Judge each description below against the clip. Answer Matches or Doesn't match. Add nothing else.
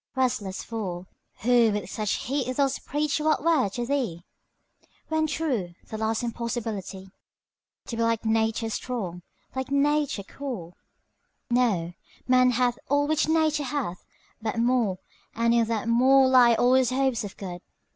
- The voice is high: Matches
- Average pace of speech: Matches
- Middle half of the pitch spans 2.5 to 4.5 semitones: Matches